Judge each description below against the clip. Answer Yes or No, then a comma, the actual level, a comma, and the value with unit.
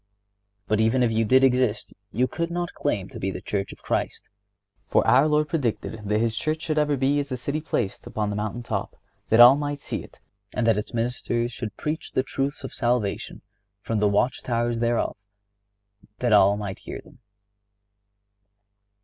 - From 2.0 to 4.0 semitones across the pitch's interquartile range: No, average, 4.5 semitones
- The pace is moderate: Yes, average, 185 wpm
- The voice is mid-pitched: No, low, 120 Hz